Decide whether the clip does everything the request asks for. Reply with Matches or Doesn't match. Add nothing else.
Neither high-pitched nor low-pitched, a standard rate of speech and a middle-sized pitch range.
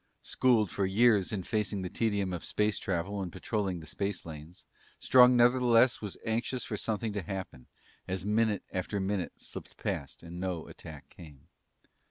Doesn't match